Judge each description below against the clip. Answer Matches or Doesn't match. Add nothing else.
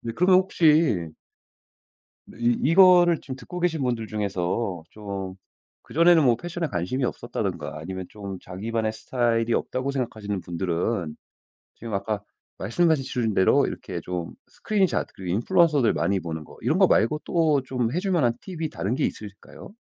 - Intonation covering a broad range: Matches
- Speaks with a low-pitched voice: Matches